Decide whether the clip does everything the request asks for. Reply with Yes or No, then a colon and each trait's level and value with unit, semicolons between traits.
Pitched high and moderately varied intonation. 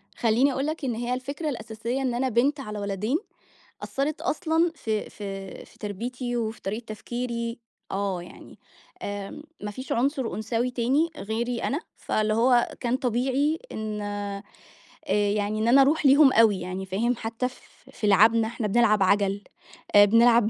Yes: high, 230 Hz; average, 3.6 semitones